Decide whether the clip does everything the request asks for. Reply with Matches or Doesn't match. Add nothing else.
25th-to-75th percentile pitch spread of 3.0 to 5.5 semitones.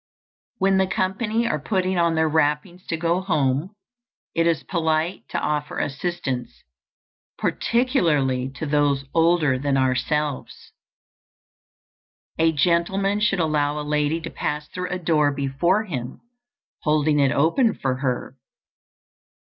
Matches